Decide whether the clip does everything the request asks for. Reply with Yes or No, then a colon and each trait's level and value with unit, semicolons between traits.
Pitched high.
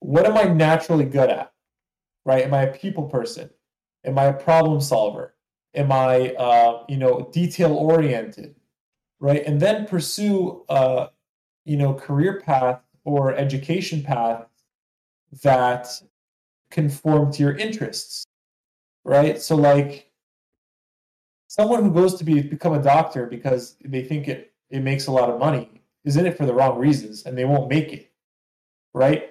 No: medium, 140 Hz